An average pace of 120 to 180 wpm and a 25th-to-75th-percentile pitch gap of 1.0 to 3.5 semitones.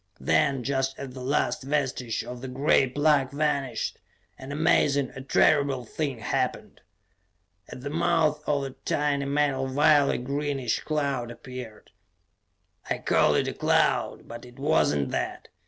Yes: average, 150 wpm; narrow, 2.4 semitones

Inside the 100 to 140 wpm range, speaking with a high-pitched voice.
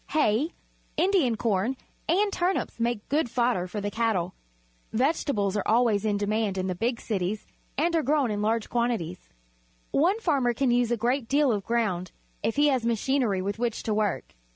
No: average, 180 wpm; high, 230 Hz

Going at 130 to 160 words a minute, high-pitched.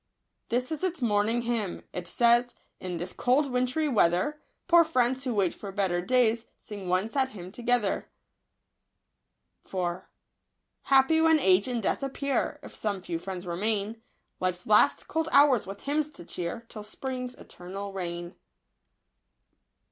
Yes: average, 145 wpm; high, 230 Hz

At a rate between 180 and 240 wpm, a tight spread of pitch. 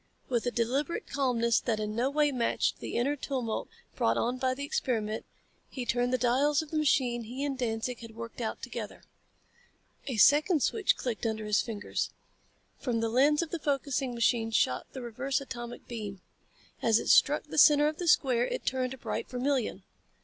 No: average, 185 wpm; average, 3.4 semitones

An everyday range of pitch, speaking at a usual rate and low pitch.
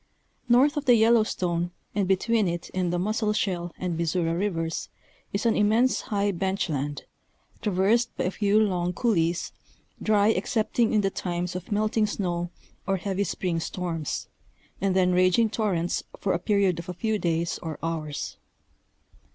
No: average, 3.6 semitones; average, 155 wpm; high, 190 Hz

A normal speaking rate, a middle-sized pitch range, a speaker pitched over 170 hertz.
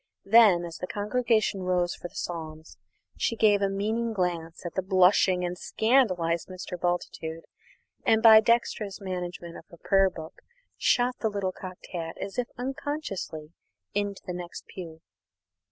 Yes: average, 155 wpm; average, 3.7 semitones; medium, 185 Hz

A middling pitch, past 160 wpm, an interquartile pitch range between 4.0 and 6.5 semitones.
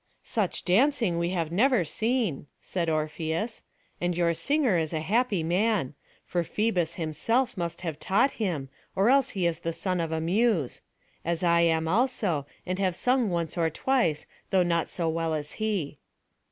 Yes: medium, 175 Hz; average, 170 wpm; average, 5.1 semitones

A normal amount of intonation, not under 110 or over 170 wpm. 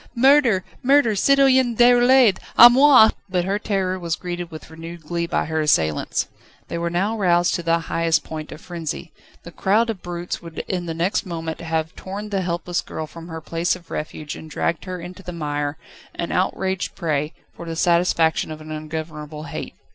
No: average, 3.3 semitones; average, 185 wpm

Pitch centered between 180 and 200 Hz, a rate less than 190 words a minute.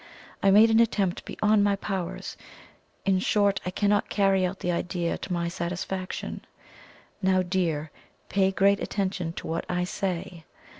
Yes: high, 190 Hz; average, 150 wpm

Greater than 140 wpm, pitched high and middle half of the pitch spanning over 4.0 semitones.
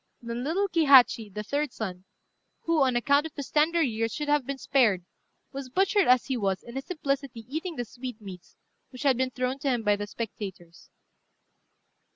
Yes: average, 185 wpm; very high, 255 Hz; average, 4.4 semitones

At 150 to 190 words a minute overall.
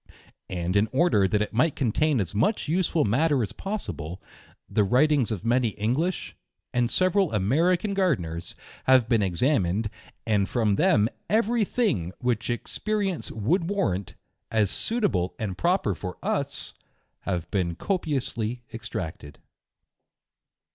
No: average, 140 wpm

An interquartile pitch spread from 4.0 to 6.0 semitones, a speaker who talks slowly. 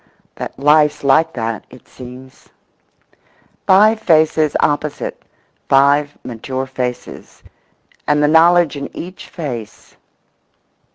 No: average, 3.5 semitones; slow, 90 wpm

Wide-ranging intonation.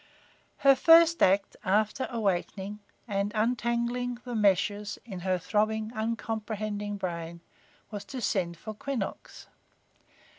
No: average, 3.1 semitones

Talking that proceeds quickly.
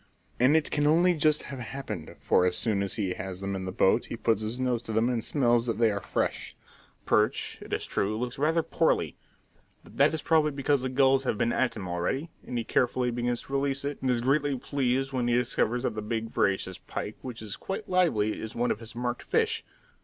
Yes: fast, 235 wpm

